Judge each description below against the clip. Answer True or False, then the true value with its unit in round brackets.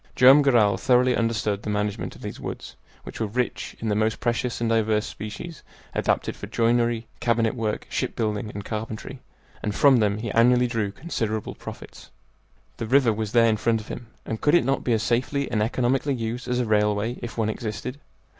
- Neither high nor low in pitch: False (115 Hz)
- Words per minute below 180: False (195 wpm)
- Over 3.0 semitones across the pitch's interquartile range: False (2.4 semitones)